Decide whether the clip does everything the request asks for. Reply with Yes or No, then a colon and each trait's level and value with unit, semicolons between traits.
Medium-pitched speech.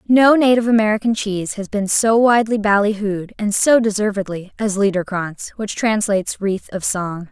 No: high, 210 Hz